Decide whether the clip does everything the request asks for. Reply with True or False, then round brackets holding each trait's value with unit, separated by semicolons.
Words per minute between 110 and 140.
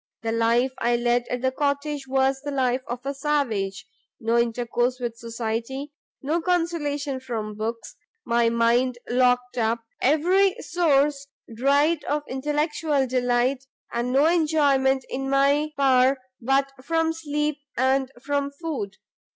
True (135 wpm)